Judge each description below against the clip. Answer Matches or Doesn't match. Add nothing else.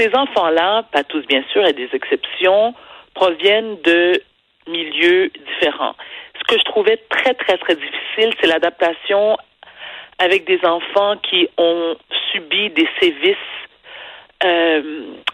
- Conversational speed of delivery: Doesn't match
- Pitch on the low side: Doesn't match